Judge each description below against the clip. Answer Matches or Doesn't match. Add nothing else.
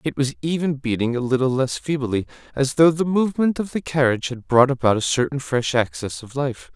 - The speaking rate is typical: Doesn't match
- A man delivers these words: Matches